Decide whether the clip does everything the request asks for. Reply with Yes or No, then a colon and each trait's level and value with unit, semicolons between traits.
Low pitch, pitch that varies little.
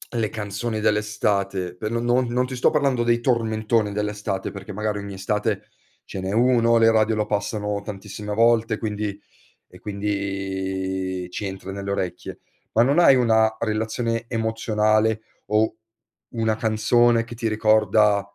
Yes: low, 110 Hz; narrow, 2.2 semitones